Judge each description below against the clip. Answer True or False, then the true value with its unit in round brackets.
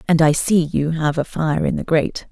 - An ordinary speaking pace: False (260 wpm)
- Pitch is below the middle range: False (160 Hz)